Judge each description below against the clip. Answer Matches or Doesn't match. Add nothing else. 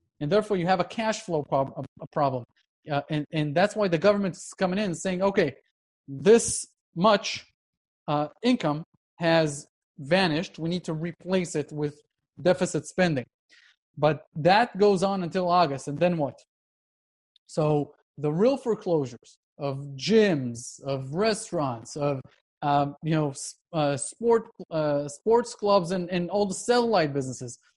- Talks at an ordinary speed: Matches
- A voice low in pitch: Doesn't match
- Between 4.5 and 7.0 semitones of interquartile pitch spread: Matches